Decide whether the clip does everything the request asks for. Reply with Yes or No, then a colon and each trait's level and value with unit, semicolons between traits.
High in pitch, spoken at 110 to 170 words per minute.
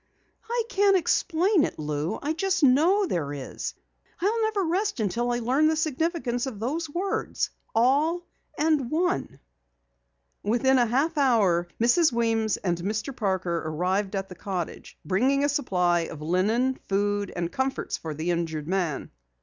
Yes: high, 240 Hz; average, 150 wpm